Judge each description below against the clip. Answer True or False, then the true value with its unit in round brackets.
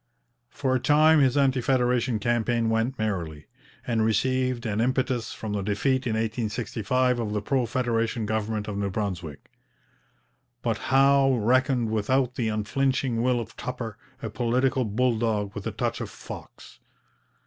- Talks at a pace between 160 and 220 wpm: False (150 wpm)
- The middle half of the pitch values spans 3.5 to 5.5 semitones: False (3.0 semitones)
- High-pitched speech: False (115 Hz)